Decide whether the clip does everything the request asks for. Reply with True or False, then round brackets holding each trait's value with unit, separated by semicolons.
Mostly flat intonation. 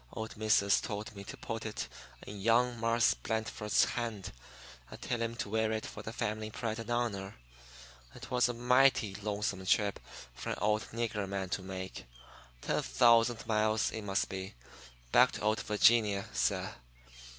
True (2.3 semitones)